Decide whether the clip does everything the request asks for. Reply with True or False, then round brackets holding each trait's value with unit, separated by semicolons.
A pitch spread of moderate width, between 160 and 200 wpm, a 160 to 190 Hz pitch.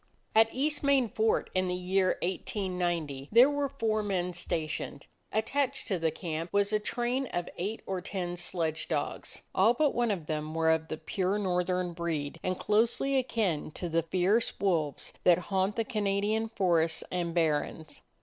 True (4.7 semitones; 170 wpm; 185 Hz)